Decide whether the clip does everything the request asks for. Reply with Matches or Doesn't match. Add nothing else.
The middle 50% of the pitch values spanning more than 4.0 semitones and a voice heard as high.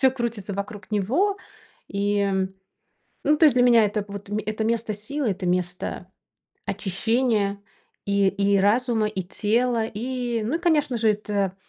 Doesn't match